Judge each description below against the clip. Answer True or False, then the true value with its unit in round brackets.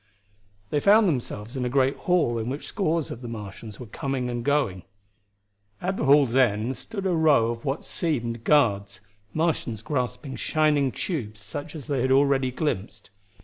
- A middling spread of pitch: True (4.4 semitones)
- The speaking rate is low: False (170 wpm)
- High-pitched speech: False (130 Hz)